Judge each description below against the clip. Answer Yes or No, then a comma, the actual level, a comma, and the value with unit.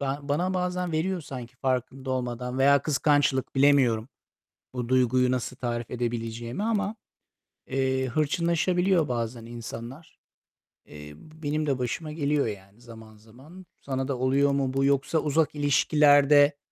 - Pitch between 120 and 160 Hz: Yes, low, 135 Hz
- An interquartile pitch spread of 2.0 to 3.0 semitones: No, average, 3.7 semitones